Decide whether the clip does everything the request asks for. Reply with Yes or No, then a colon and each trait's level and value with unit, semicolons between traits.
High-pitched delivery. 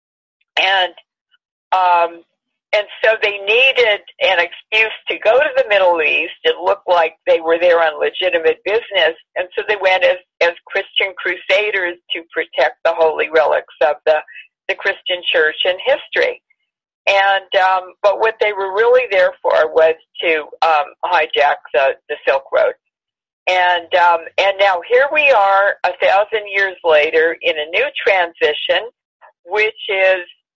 Yes: high, 195 Hz